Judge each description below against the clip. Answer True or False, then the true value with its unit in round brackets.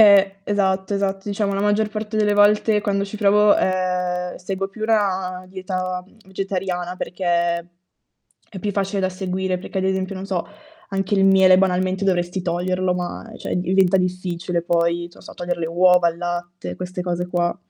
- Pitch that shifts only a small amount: True (1.7 semitones)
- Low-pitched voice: False (185 Hz)